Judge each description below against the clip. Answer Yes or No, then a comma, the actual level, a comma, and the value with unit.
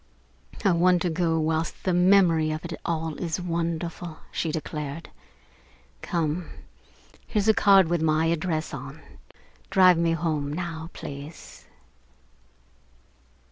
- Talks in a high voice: No, medium, 165 Hz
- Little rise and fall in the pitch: Yes, narrow, 1.9 semitones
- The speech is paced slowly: Yes, slow, 120 wpm